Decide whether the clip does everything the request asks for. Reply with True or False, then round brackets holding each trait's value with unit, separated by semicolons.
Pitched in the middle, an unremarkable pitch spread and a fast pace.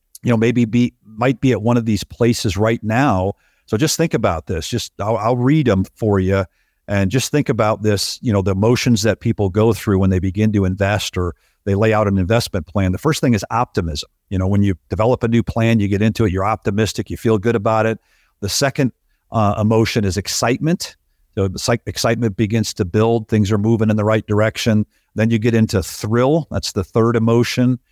False (110 Hz; 3.0 semitones; 215 wpm)